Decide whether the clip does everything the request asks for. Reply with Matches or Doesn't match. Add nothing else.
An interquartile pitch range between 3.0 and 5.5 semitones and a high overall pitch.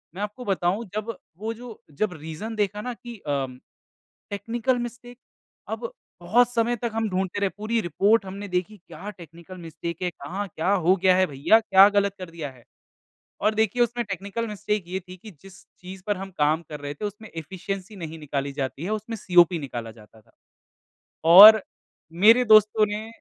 Matches